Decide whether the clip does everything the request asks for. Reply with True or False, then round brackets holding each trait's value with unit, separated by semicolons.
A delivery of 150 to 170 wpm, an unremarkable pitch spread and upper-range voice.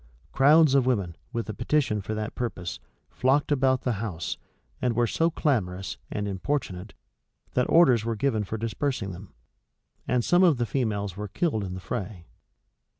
False (165 wpm; 5.0 semitones; 115 Hz)